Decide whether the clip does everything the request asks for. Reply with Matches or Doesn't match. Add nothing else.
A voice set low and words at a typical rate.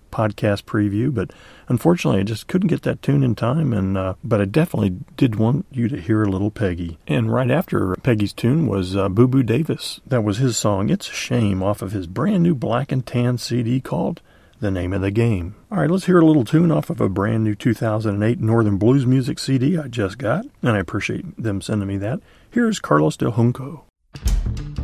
Doesn't match